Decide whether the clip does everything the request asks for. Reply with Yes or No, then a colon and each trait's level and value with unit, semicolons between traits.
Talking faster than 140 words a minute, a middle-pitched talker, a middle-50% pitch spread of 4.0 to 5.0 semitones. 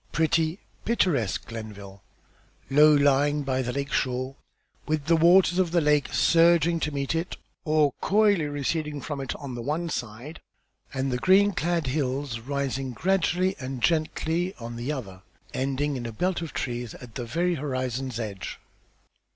Yes: average, 160 wpm; medium, 145 Hz; average, 4.4 semitones